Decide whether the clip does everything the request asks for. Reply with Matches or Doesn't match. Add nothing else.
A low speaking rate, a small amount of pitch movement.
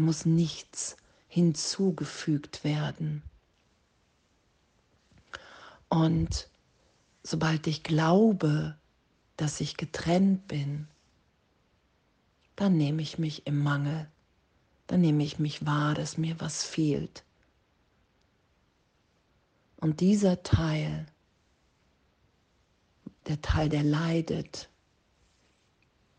Matches